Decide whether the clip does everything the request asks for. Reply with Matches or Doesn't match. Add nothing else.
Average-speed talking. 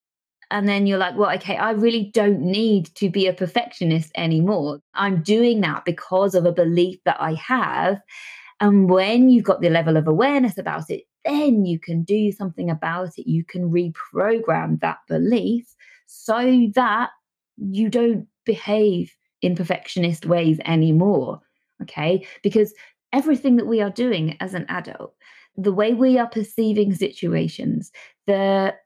Matches